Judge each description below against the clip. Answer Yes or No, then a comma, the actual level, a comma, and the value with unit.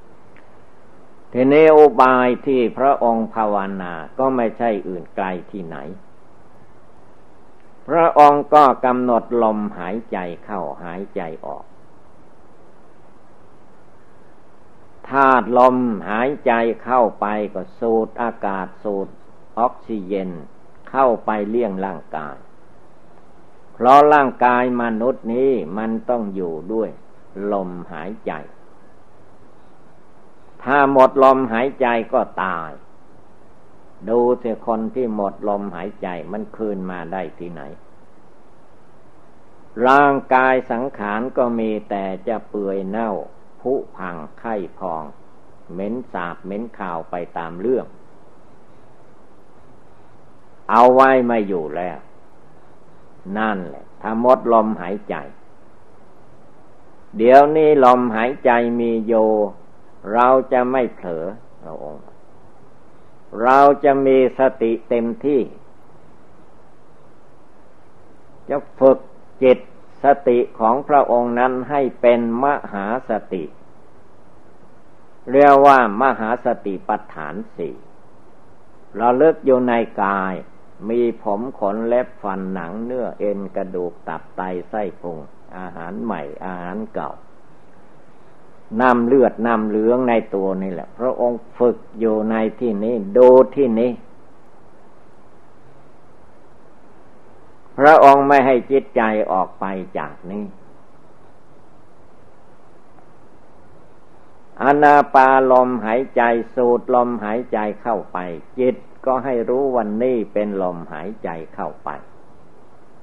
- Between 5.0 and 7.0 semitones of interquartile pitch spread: No, average, 3.9 semitones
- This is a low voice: Yes, low, 120 Hz